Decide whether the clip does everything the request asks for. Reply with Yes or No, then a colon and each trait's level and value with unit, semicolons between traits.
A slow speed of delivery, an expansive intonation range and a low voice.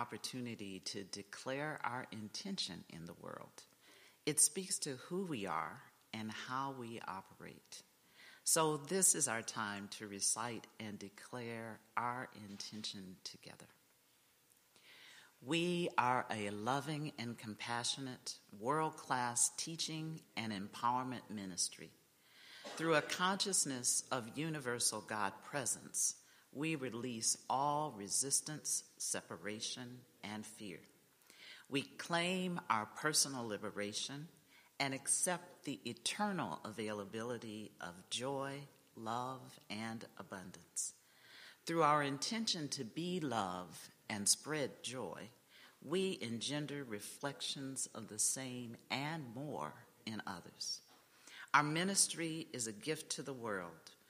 Yes: slow, 110 wpm; wide, 5.8 semitones; low, 125 Hz